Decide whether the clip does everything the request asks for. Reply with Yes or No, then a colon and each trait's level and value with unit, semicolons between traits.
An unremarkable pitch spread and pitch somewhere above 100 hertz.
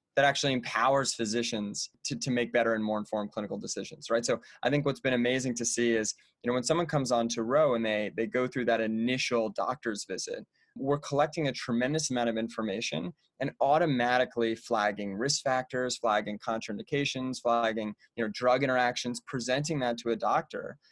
No: narrow, 2.3 semitones; low, 120 Hz